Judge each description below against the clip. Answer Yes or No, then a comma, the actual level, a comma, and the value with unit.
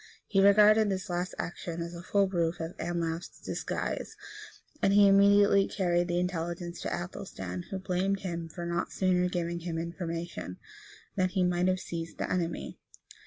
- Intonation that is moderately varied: No, narrow, 2.1 semitones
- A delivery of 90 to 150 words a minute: No, average, 165 wpm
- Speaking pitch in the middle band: Yes, medium, 175 Hz